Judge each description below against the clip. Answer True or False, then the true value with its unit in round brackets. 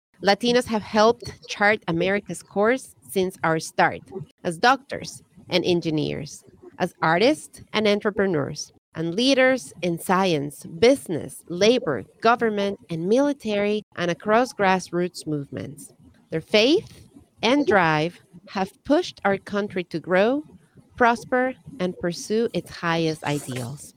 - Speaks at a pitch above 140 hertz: True (190 Hz)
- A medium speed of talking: False (115 wpm)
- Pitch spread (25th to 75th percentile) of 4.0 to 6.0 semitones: True (4.9 semitones)